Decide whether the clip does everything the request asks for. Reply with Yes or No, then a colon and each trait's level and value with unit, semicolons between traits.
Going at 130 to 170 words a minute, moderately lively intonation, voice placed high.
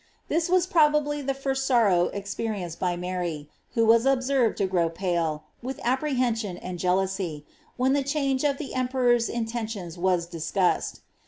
No: average, 150 wpm; wide, 6.9 semitones; high, 225 Hz